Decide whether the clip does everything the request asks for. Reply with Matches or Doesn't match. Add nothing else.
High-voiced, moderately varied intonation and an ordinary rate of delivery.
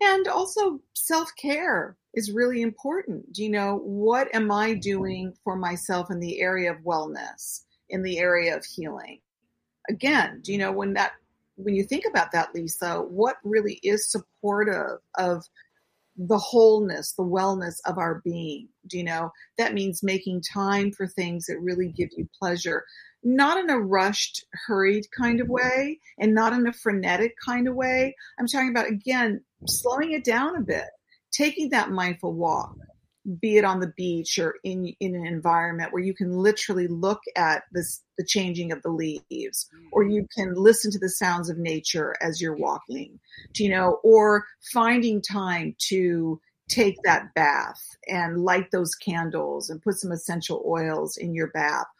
Matches